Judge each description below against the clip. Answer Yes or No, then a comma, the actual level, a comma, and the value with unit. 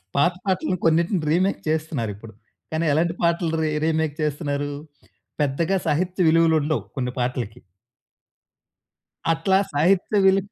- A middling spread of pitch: Yes, average, 3.2 semitones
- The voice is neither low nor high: Yes, medium, 160 Hz